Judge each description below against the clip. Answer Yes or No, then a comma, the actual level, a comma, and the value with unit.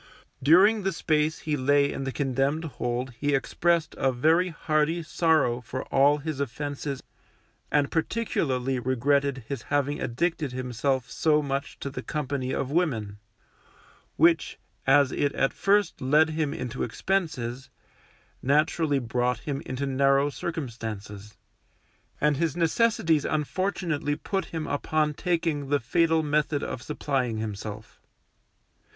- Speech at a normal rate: No, slow, 130 wpm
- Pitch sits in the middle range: Yes, medium, 145 Hz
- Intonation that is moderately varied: Yes, average, 3.5 semitones